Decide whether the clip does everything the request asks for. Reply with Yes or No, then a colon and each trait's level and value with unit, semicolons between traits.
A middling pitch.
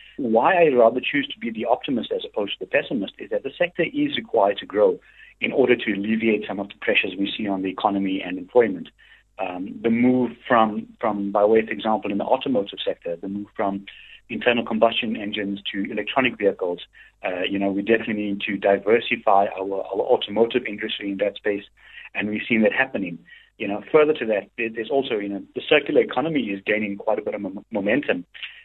No: low, 110 Hz